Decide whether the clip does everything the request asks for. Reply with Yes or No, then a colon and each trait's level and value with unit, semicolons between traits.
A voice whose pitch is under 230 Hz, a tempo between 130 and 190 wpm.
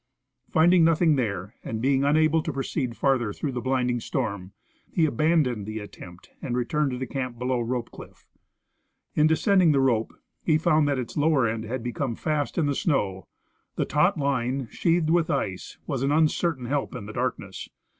Yes: low, 135 Hz; average, 185 wpm